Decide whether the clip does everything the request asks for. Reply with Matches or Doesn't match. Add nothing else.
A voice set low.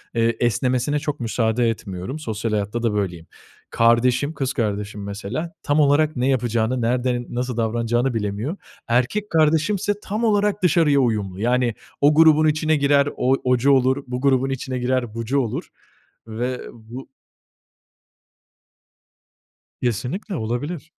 Matches